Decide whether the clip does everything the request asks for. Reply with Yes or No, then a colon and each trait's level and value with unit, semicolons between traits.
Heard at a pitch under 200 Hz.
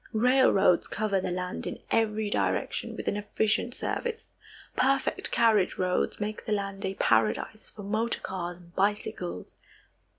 No: high, 205 Hz